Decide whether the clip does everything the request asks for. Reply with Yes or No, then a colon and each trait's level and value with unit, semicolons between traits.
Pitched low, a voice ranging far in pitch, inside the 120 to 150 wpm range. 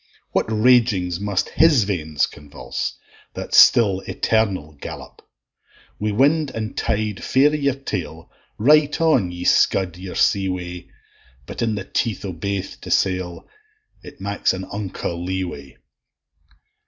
No: low, 100 Hz; average, 4.4 semitones; average, 140 wpm